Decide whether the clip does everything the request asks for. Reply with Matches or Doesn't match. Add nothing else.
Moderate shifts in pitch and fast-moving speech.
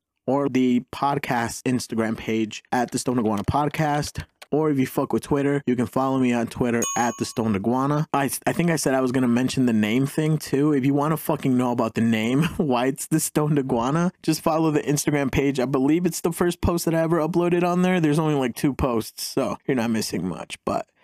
Matches